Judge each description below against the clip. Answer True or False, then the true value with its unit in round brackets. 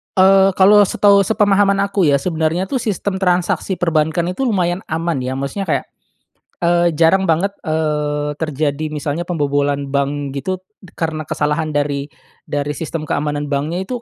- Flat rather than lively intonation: False (4.3 semitones)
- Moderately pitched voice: True (160 Hz)